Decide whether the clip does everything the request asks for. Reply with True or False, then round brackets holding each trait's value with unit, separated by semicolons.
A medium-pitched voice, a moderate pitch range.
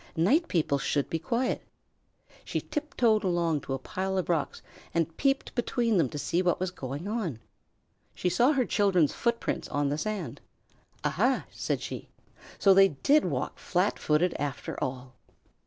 False (180 Hz; 6.8 semitones)